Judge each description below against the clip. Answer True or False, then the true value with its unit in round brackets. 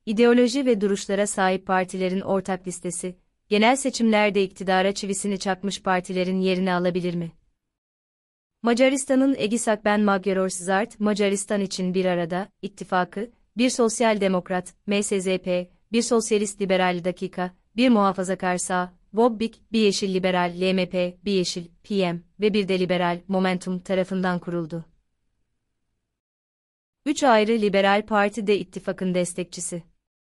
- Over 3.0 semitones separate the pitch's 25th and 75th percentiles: False (2.5 semitones)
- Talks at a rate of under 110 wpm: False (115 wpm)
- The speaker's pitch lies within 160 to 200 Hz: True (190 Hz)